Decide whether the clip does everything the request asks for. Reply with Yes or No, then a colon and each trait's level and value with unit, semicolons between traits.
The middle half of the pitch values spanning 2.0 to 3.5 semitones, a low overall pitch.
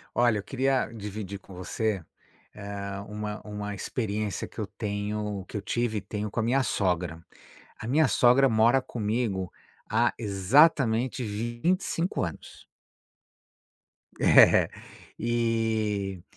Yes: average, 2.8 semitones; low, 110 Hz